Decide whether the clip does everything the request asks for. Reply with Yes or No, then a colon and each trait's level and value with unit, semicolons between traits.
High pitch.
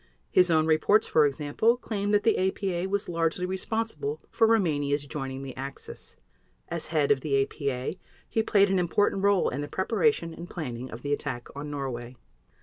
No: medium, 160 Hz